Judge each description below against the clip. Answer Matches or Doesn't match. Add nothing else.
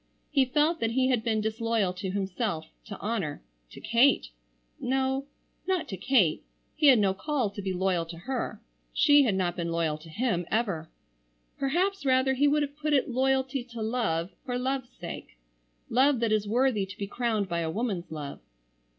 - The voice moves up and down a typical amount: Doesn't match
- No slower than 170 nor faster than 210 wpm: Matches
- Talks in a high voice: Matches